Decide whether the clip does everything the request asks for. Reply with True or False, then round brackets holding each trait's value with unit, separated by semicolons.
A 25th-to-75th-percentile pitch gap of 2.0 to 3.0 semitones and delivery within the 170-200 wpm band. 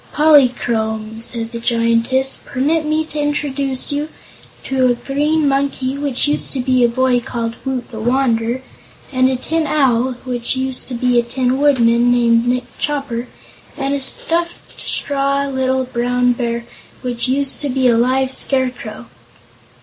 False (2.6 semitones; 155 wpm)